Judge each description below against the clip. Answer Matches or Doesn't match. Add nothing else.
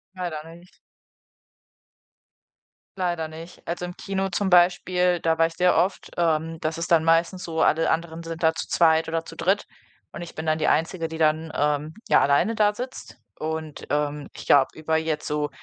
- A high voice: Doesn't match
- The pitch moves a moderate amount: Doesn't match